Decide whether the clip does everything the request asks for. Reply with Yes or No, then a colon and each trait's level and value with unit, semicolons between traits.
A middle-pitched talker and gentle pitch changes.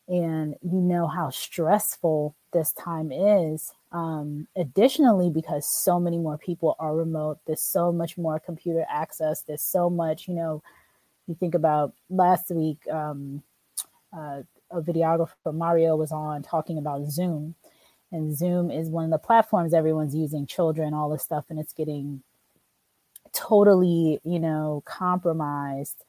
Yes: medium, 160 Hz; narrow, 2.2 semitones